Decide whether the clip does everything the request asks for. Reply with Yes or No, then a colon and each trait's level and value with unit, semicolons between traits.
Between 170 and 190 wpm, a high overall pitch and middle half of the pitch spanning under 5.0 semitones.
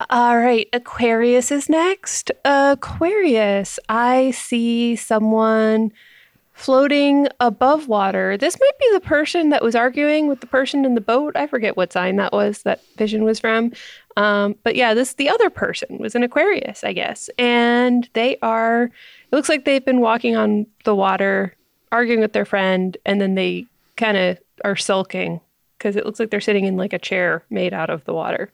Yes: average, 180 wpm; high, 235 Hz; average, 4.5 semitones